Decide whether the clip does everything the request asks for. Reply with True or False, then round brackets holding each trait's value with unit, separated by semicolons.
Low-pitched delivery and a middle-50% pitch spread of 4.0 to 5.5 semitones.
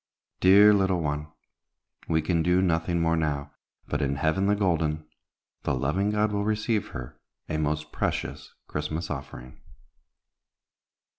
True (80 Hz; 4.4 semitones)